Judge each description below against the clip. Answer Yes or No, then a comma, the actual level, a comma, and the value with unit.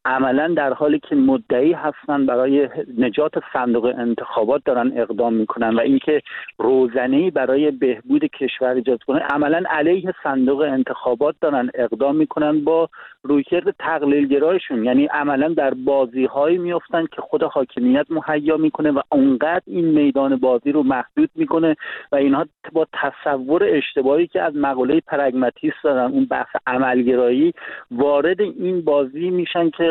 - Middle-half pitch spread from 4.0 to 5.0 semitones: Yes, average, 4.5 semitones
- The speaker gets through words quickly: No, average, 140 wpm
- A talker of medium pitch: Yes, medium, 150 Hz